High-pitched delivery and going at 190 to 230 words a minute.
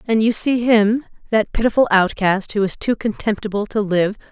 No: high, 215 Hz; average, 180 wpm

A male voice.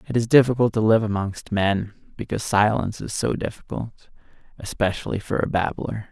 Yes: male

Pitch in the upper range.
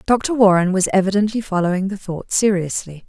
Yes: high, 195 Hz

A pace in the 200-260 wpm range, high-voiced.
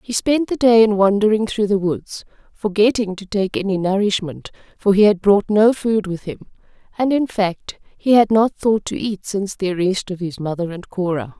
Yes: fast, 205 wpm; high, 200 Hz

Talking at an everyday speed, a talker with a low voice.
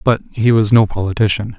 Yes: average, 190 wpm; low, 110 Hz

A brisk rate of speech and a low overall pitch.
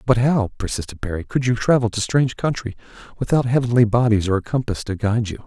Yes: fast, 210 wpm; low, 115 Hz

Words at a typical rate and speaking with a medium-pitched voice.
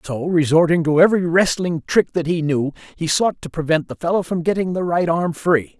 No: fast, 215 wpm; medium, 165 Hz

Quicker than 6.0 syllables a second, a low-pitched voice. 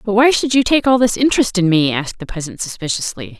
No: 6.4 syllables/s; high, 205 Hz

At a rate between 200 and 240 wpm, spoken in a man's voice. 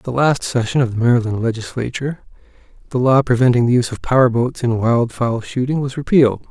Yes: fast, 205 wpm; male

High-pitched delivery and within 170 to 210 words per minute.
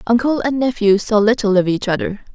Yes: high, 220 Hz; fast, 205 wpm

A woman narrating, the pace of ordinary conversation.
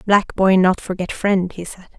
No: female; fast, 210 wpm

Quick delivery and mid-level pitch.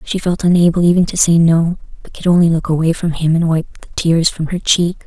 Yes: fast, 250 wpm; medium, 170 Hz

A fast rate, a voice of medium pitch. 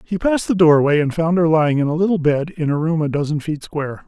Yes: fast, 280 wpm; medium, 160 Hz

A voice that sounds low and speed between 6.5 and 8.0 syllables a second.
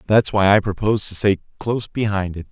Yes: low, 100 Hz; 6.6 syllables/s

